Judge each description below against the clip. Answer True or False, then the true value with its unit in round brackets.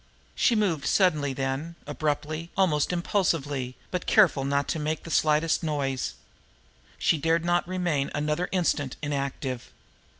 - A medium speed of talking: False (130 wpm)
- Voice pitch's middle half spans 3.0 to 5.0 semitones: True (3.4 semitones)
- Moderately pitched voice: True (155 Hz)